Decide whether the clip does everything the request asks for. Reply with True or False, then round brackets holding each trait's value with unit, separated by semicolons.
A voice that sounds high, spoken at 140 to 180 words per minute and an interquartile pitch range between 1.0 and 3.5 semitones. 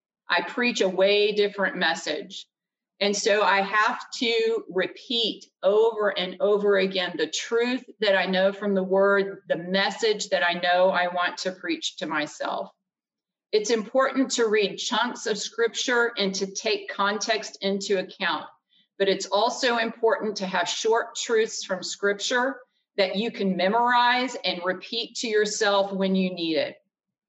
True (200 Hz; 155 wpm; 3.2 semitones)